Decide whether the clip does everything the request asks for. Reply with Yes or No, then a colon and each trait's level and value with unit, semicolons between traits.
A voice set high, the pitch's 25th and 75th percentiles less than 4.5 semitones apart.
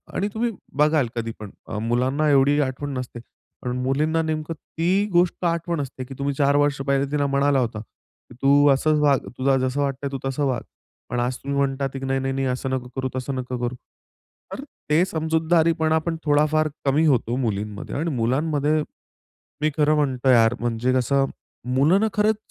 No: medium, 140 Hz; average, 3.2 semitones